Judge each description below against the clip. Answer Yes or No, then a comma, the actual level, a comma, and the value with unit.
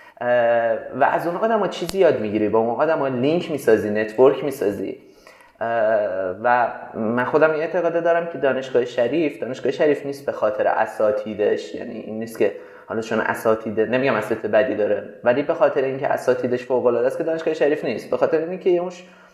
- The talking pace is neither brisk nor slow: No, fast, 175 wpm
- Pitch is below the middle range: Yes, low, 130 Hz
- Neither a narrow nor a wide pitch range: No, wide, 6.6 semitones